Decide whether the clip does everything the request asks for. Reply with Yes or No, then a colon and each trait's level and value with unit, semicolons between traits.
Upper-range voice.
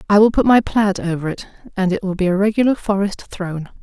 Yes: high, 195 Hz